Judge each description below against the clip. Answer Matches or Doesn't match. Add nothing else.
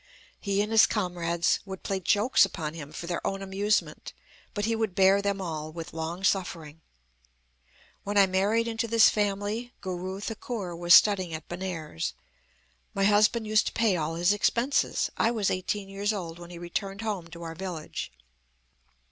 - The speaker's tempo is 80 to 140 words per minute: Doesn't match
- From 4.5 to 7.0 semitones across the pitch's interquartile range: Doesn't match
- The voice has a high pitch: Matches